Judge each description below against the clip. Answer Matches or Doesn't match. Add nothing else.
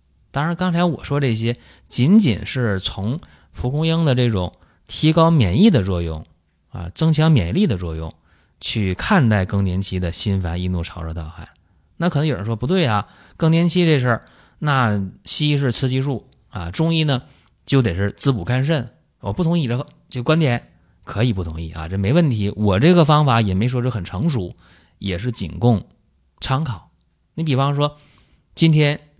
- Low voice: Matches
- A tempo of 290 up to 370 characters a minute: Doesn't match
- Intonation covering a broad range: Matches